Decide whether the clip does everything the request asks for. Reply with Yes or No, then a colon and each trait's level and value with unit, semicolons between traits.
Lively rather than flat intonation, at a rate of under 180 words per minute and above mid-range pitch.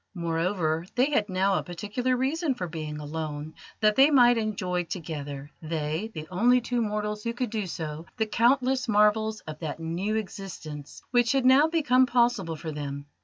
Yes: wide, 7.1 semitones; average, 170 wpm; high, 205 Hz